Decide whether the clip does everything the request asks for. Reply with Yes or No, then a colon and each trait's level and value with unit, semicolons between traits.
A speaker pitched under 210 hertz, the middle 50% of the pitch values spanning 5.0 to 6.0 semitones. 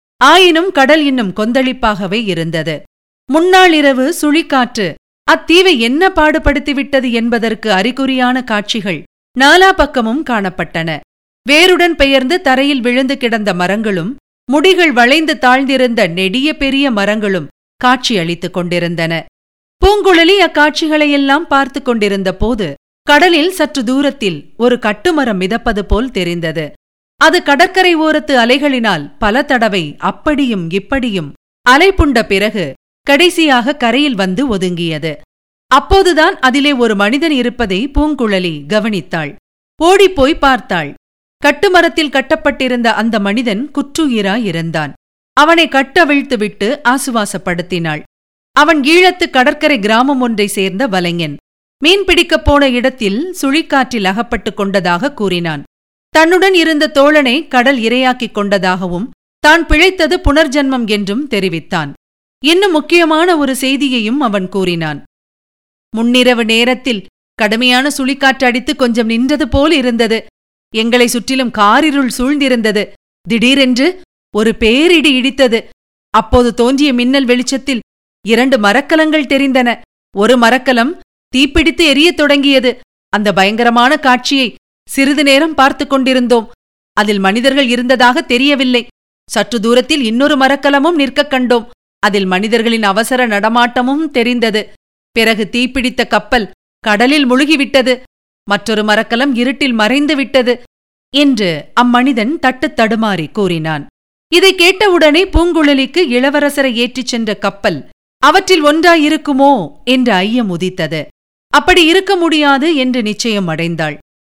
No: very high, 255 Hz; wide, 5.4 semitones